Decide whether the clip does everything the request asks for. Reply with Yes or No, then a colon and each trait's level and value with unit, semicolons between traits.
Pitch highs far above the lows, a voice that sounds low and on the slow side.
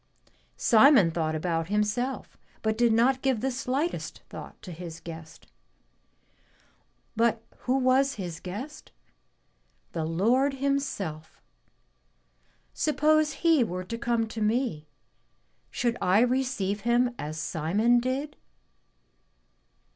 No: wide, 6.5 semitones; high, 230 Hz; slow, 110 wpm